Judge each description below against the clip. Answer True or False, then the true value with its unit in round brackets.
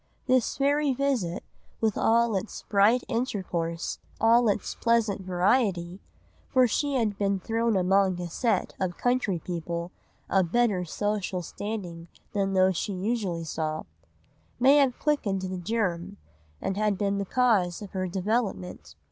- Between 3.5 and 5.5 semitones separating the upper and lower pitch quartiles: True (4.6 semitones)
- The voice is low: False (200 Hz)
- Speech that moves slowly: True (130 wpm)